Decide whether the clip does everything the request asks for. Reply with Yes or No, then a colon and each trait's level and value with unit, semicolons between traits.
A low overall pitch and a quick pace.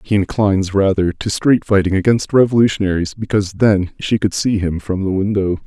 No: low, 100 Hz; average, 170 wpm